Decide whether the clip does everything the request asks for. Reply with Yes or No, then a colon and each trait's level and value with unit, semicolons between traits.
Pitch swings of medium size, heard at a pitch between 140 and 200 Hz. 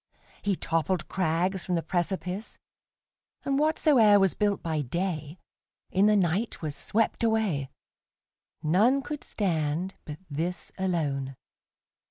Yes: average, 4.5 semitones; medium, 185 Hz